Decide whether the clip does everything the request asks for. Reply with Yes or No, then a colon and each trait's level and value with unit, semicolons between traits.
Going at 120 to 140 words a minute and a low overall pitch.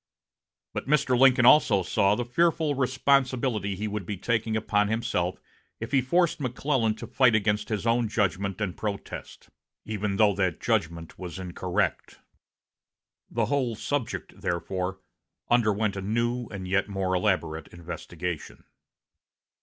Yes: slow, 135 wpm; low, 105 Hz